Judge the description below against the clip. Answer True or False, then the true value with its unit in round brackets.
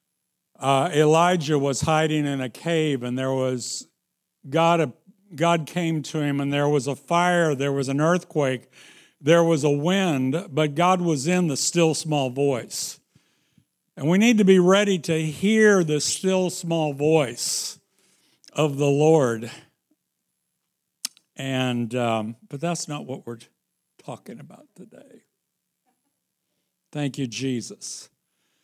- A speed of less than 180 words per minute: True (135 wpm)